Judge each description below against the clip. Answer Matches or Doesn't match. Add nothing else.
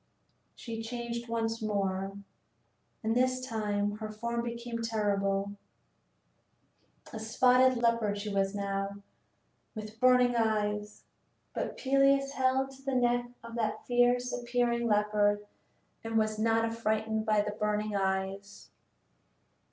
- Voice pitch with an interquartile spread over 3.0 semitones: Doesn't match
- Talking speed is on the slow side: Matches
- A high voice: Matches